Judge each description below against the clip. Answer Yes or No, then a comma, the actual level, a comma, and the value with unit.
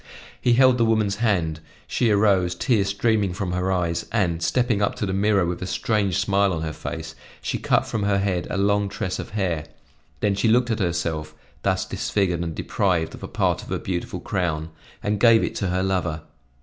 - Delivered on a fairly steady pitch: No, average, 3.2 semitones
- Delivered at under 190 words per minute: No, fast, 205 wpm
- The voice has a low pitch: Yes, very low, 95 Hz